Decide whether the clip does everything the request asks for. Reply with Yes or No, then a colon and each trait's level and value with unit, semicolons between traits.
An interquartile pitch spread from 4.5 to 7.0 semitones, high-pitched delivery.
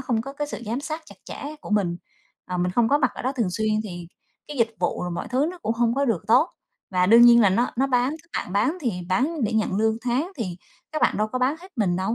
Yes: average, 4.8 semitones; high, 235 Hz